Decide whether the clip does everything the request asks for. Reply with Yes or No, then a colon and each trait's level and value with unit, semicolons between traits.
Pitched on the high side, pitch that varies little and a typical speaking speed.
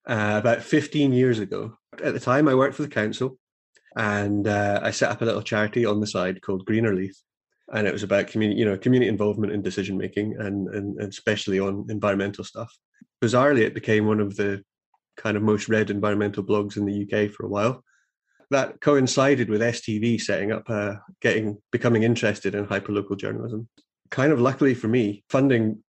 No: low, 105 Hz; narrow, 2.2 semitones; average, 190 wpm